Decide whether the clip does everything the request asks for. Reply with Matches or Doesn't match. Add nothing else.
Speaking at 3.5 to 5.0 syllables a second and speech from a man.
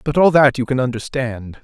Doesn't match